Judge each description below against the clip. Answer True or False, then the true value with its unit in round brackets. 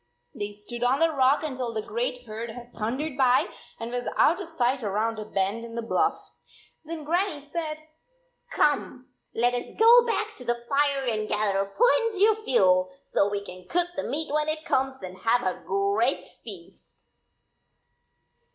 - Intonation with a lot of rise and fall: True (6.5 semitones)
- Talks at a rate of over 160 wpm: True (175 wpm)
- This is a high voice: True (250 Hz)